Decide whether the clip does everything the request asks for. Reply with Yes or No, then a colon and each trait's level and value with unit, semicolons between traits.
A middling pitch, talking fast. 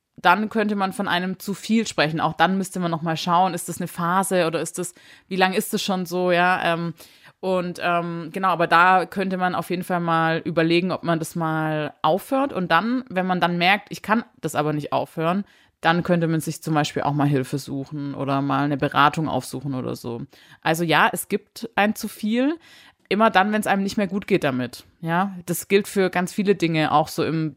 Yes: medium, 175 Hz; fast, 220 wpm